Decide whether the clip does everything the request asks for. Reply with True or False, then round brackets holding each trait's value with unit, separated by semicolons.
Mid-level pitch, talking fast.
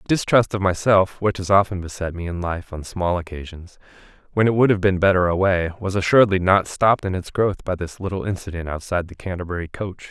False (95 Hz; 215 wpm)